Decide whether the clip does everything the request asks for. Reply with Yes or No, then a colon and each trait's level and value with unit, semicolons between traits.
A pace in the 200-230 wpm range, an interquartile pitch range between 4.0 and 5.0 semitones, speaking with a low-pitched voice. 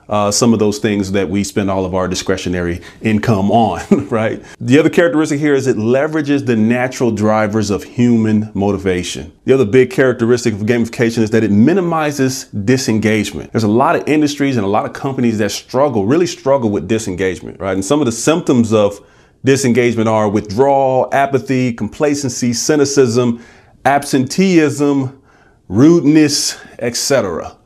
No: average, 155 wpm; average, 4.6 semitones; low, 120 Hz